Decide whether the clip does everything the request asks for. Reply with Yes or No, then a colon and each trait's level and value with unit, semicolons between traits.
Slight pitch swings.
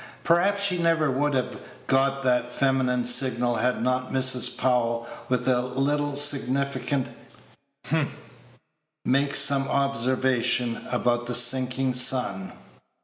Yes: narrow, 1.9 semitones